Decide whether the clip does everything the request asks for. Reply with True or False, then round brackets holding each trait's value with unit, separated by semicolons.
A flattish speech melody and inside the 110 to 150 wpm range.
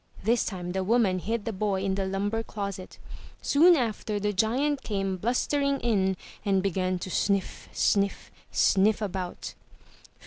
False (3.0 semitones; 145 wpm)